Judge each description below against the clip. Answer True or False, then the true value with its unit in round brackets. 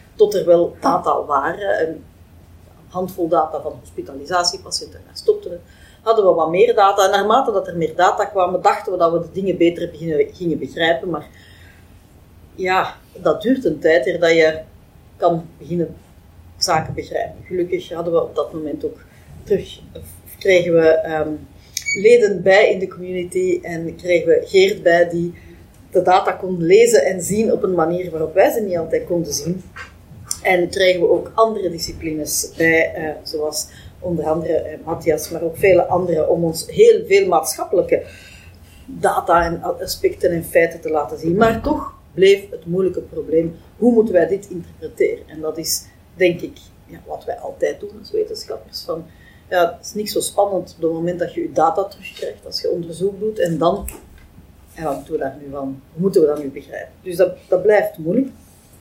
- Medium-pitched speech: True (175 Hz)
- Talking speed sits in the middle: True (180 wpm)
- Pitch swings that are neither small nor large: True (4.2 semitones)